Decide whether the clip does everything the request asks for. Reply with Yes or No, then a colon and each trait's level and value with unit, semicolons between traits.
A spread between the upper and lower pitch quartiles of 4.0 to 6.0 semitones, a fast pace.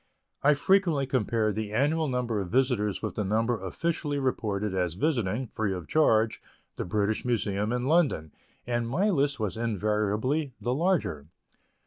No: average, 4.9 semitones; average, 150 wpm